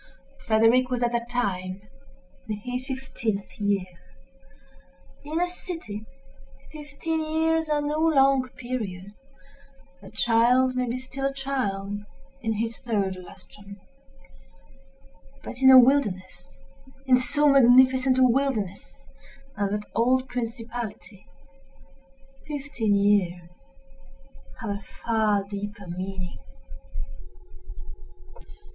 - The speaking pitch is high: Yes, high, 240 Hz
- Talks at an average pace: No, slow, 100 wpm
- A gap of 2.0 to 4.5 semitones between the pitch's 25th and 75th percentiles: No, average, 4.9 semitones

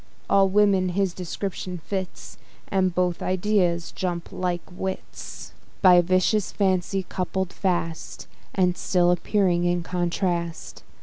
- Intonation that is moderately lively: No, narrow, 1.5 semitones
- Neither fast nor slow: No, slow, 115 wpm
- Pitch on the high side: No, medium, 180 Hz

